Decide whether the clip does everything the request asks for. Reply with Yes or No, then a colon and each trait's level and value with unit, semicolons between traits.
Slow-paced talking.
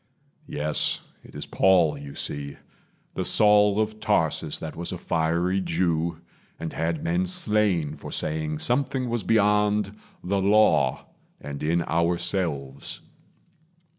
Yes: slow, 125 wpm